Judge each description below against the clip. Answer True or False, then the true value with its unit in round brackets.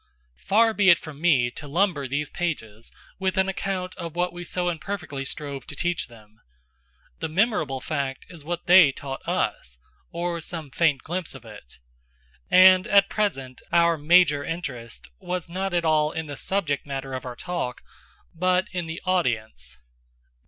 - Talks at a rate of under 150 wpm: False (165 wpm)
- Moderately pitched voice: True (165 Hz)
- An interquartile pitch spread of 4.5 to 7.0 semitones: True (5.0 semitones)